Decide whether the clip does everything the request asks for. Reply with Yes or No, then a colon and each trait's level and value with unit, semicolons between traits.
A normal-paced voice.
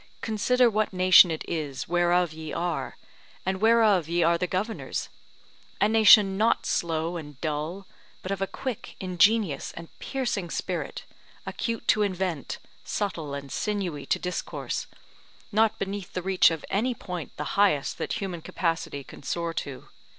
Yes: average, 150 wpm